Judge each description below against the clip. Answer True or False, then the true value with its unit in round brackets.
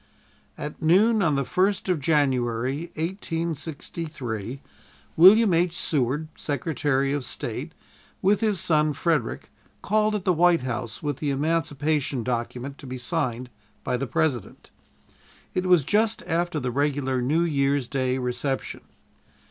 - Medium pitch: True (150 Hz)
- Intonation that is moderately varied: True (4.7 semitones)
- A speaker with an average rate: False (130 wpm)